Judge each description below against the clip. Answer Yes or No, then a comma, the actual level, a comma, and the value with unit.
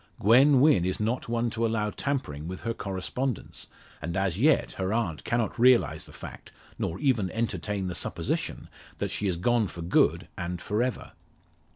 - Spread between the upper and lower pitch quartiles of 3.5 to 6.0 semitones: Yes, average, 4.5 semitones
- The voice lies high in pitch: No, low, 110 Hz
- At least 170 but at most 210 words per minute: Yes, average, 175 wpm